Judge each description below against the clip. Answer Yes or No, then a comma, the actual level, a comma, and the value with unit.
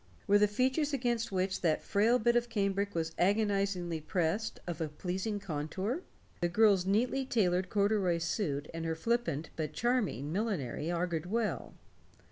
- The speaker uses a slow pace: No, average, 150 wpm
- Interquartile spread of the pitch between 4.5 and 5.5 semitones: Yes, average, 4.8 semitones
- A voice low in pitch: No, high, 195 Hz